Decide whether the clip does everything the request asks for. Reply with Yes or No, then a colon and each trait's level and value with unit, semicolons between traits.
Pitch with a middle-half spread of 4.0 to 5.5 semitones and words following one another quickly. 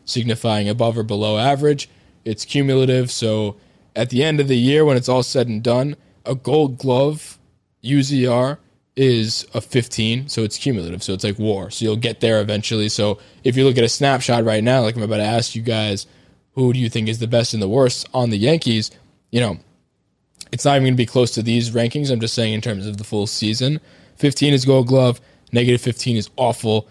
No: average, 3.3 semitones; fast, 215 wpm